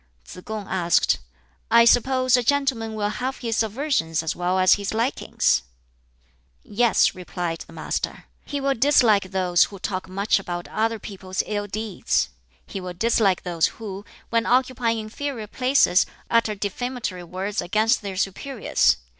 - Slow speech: No, average, 145 wpm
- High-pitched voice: Yes, high, 210 Hz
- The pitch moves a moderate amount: Yes, average, 4.2 semitones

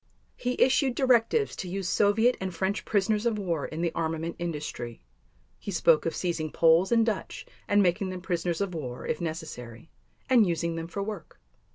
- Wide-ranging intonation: No, average, 4.2 semitones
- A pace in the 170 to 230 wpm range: Yes, average, 180 wpm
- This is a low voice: No, medium, 180 Hz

